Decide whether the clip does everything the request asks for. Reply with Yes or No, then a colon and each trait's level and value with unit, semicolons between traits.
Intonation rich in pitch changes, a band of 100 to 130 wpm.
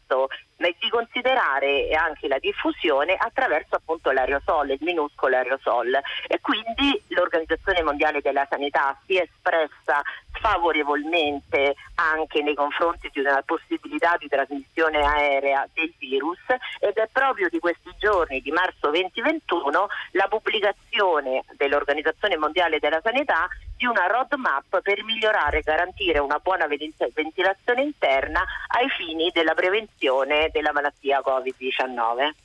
Yes: wide, 5.7 semitones; average, 120 wpm